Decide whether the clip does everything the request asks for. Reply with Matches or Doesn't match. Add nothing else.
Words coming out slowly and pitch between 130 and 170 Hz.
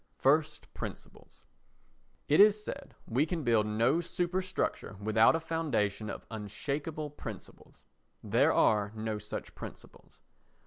Matches